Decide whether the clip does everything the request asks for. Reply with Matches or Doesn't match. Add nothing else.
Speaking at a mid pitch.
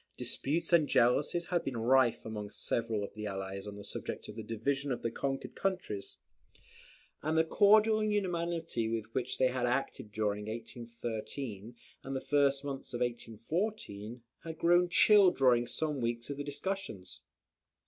Doesn't match